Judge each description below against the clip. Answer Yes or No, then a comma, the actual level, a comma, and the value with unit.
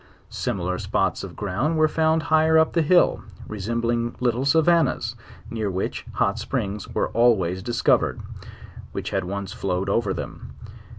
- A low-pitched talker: Yes, low, 115 Hz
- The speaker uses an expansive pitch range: Yes, wide, 7.9 semitones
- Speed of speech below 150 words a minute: Yes, average, 140 wpm